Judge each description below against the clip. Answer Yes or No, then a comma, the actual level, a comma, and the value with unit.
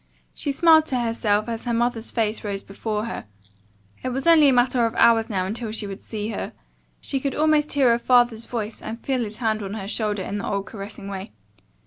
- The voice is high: Yes, high, 225 Hz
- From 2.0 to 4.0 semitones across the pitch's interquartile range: Yes, average, 3.0 semitones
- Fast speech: Yes, fast, 215 wpm